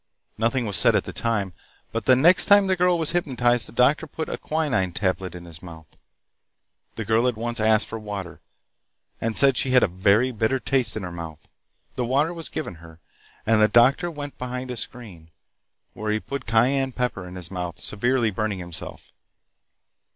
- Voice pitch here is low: Yes, low, 115 Hz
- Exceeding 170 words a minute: Yes, average, 190 wpm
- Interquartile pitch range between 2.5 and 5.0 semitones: No, wide, 5.4 semitones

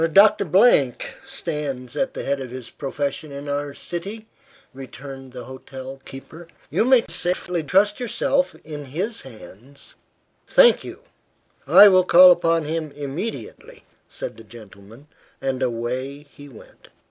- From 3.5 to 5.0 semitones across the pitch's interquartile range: No, wide, 5.5 semitones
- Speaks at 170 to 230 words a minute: No, slow, 135 wpm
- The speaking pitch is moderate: Yes, medium, 145 Hz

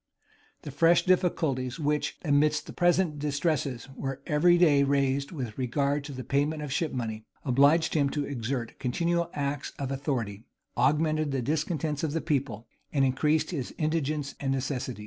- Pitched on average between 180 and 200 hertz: No, medium, 145 Hz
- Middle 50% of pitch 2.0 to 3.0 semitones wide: Yes, average, 2.7 semitones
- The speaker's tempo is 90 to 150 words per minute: No, average, 160 wpm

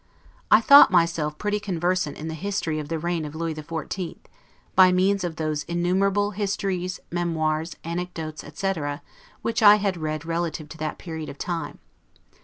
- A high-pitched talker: No, medium, 170 Hz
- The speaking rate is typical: Yes, average, 160 wpm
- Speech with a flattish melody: No, average, 3.3 semitones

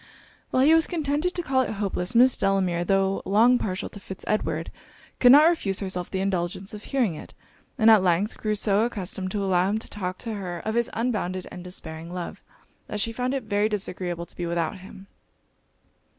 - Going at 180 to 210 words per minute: Yes, average, 200 wpm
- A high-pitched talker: Yes, high, 200 Hz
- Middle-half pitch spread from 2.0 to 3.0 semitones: No, average, 4.0 semitones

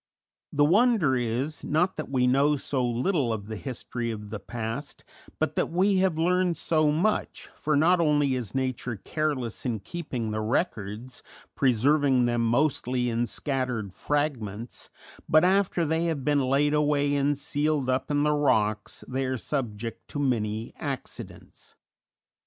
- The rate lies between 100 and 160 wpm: Yes, average, 150 wpm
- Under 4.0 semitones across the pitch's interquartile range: No, average, 4.3 semitones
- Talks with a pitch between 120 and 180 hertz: Yes, low, 135 Hz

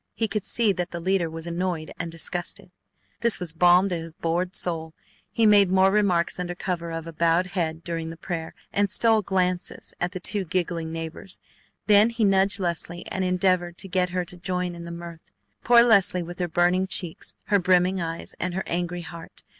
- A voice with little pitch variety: Yes, narrow, 2.1 semitones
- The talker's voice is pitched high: No, medium, 180 Hz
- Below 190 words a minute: No, average, 200 wpm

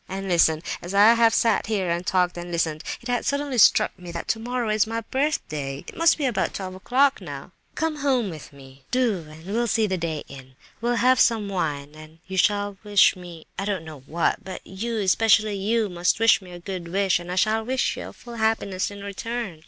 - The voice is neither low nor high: No, high, 195 Hz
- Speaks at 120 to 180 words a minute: No, fast, 205 wpm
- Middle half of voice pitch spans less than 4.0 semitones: No, average, 4.8 semitones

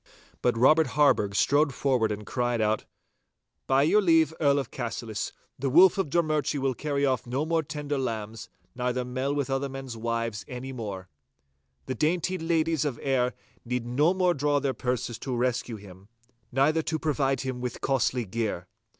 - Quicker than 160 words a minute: Yes, average, 170 wpm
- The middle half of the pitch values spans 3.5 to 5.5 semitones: Yes, average, 3.9 semitones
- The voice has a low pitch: Yes, low, 130 Hz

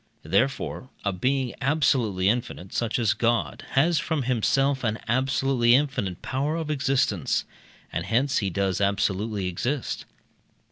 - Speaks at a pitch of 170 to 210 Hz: No, low, 120 Hz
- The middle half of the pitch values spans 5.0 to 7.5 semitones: Yes, average, 5.3 semitones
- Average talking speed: No, slow, 130 wpm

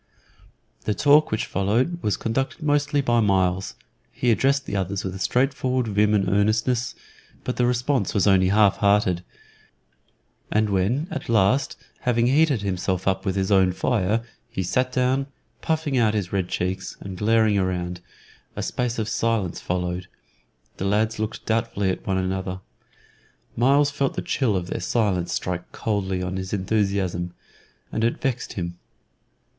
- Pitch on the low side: Yes, low, 105 Hz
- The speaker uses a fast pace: No, average, 155 wpm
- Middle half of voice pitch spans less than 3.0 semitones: No, average, 4.7 semitones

